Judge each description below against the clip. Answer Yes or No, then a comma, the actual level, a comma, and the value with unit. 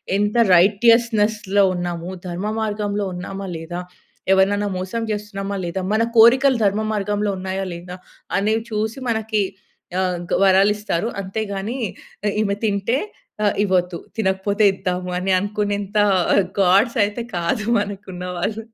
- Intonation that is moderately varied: No, narrow, 2.2 semitones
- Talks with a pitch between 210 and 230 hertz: No, high, 200 Hz